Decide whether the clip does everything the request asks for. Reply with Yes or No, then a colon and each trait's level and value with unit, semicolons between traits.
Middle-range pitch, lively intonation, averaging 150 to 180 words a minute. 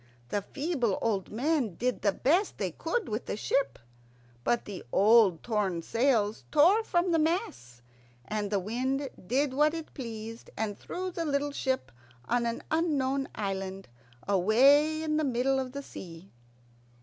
No: very high, 250 Hz; wide, 6.3 semitones; average, 155 wpm